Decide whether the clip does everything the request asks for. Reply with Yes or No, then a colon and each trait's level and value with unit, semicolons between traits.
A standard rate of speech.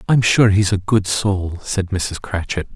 Yes: average, 195 wpm